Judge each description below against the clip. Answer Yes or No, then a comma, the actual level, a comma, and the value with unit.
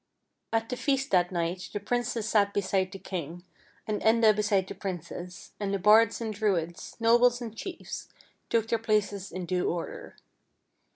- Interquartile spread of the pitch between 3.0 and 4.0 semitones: Yes, average, 3.6 semitones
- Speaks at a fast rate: No, average, 165 wpm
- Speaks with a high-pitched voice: Yes, high, 205 Hz